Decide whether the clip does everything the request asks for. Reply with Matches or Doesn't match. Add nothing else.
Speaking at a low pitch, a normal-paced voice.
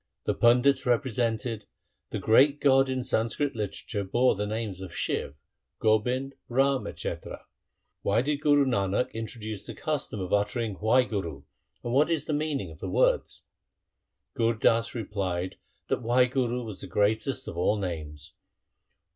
Matches